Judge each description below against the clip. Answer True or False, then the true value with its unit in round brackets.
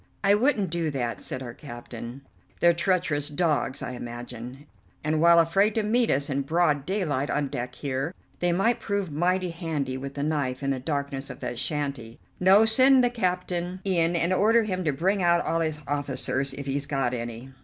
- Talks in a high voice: False (155 Hz)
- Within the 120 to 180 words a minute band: False (190 wpm)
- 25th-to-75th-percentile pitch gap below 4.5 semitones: False (5.2 semitones)